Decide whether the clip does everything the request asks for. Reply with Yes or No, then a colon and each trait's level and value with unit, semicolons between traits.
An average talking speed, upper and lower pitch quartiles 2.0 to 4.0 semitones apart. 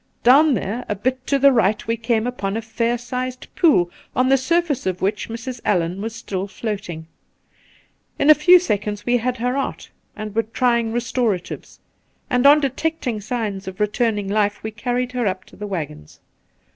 Yes: average, 185 wpm; average, 3.5 semitones